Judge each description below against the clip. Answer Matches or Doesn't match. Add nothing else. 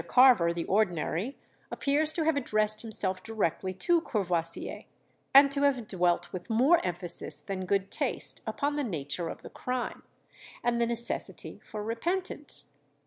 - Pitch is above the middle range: Matches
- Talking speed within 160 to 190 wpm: Doesn't match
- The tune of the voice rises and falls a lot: Matches